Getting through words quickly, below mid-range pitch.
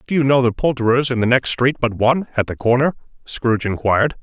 Yes: fast, 225 wpm; low, 125 Hz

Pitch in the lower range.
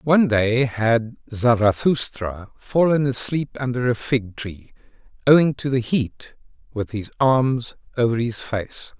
Yes: low, 120 Hz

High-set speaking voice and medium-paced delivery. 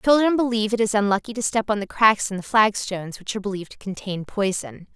No: high, 210 Hz; fast, 230 wpm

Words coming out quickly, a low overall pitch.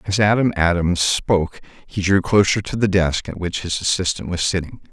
No: average, 195 wpm; very low, 90 Hz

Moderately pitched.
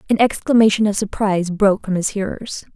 No: high, 205 Hz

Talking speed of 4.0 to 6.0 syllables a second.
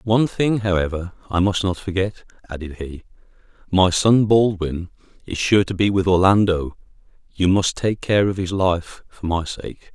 Yes: 4.7 syllables/s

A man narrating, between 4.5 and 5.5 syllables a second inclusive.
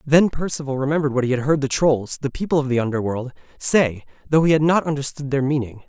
No: male; 6.3 syllables/s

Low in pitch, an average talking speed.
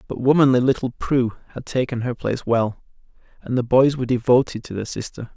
Yes: low, 125 Hz; average, 190 wpm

